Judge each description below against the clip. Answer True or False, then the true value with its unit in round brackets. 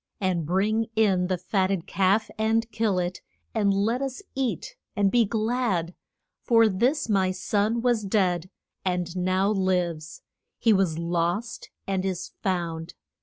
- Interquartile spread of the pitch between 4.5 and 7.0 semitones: False (3.5 semitones)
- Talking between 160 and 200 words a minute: False (145 wpm)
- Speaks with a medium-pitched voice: False (195 Hz)